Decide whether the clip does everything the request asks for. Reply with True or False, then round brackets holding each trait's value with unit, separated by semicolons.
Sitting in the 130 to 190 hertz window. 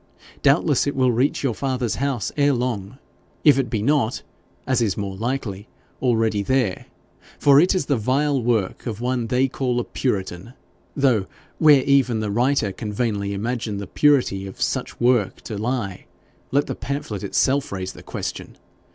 False (120 Hz)